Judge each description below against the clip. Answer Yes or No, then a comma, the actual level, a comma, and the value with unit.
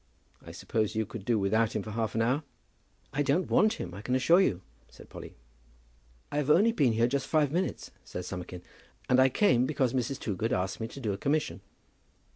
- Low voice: Yes, low, 120 Hz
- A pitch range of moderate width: Yes, average, 4.9 semitones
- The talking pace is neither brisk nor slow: No, fast, 210 wpm